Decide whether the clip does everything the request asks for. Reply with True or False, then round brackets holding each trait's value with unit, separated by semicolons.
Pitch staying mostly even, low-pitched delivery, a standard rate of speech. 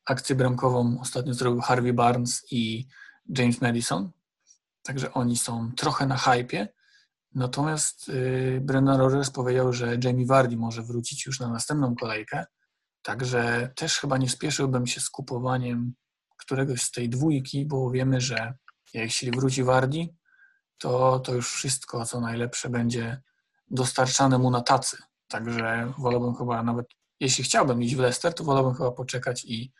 True (1.8 semitones; 125 Hz; 145 wpm)